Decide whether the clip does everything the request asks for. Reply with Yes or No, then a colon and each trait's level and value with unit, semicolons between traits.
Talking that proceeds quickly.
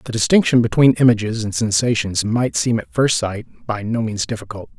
No: average, 190 wpm